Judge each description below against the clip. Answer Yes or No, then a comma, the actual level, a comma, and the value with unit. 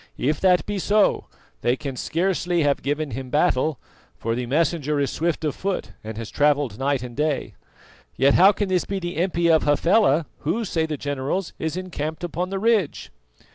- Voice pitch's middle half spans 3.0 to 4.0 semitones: No, average, 4.4 semitones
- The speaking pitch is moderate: Yes, medium, 155 Hz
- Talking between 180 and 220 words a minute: Yes, average, 185 wpm